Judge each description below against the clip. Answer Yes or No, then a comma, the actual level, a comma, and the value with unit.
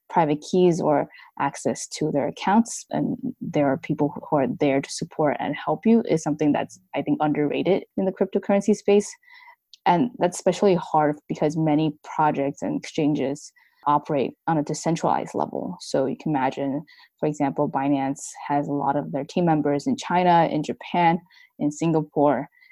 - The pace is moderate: Yes, average, 165 wpm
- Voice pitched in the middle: Yes, medium, 155 Hz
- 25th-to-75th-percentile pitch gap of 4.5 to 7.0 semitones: Yes, average, 4.8 semitones